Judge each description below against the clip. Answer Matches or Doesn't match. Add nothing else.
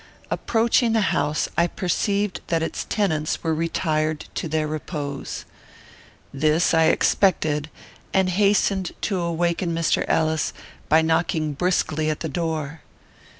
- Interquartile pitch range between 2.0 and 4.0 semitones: Matches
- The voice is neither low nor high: Matches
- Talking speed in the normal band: Doesn't match